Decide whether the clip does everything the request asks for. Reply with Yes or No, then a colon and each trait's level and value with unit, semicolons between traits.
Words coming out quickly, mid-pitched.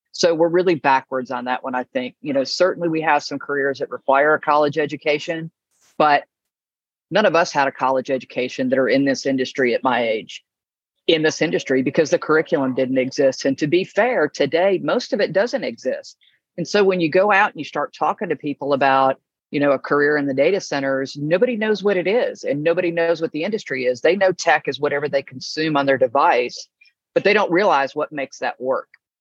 Yes: fast, 220 wpm; medium, 150 Hz